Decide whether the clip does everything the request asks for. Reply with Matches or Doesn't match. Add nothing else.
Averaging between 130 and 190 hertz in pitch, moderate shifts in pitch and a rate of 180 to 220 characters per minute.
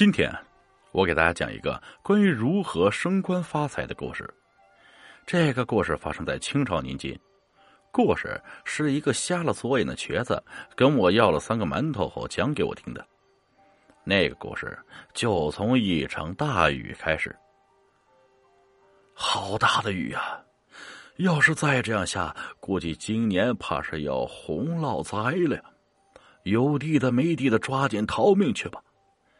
Doesn't match